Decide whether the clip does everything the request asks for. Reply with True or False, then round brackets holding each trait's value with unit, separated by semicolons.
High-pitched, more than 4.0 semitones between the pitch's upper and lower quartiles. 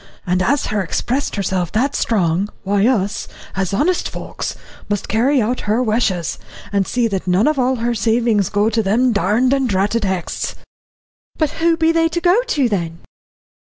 True (220 Hz; 4.9 semitones)